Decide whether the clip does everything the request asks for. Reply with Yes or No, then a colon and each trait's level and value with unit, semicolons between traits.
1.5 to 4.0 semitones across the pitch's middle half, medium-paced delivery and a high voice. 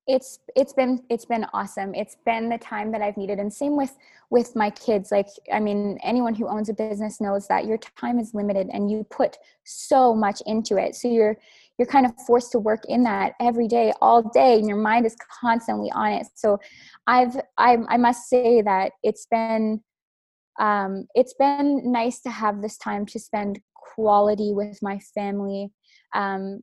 Yes: average, 2.7 semitones; average, 190 wpm; high, 220 Hz